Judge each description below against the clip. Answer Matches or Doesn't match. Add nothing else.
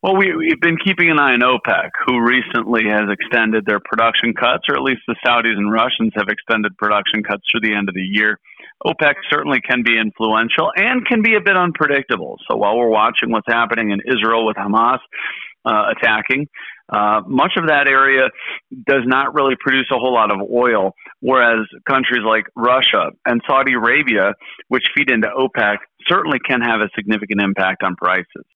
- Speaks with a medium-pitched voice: Doesn't match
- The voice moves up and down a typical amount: Matches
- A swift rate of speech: Doesn't match